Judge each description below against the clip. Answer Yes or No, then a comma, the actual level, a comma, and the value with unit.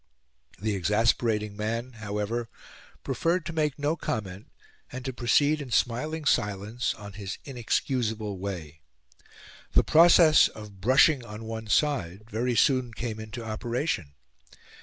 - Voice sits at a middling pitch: No, low, 115 Hz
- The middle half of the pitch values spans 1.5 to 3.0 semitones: No, average, 3.8 semitones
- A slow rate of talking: Yes, slow, 125 wpm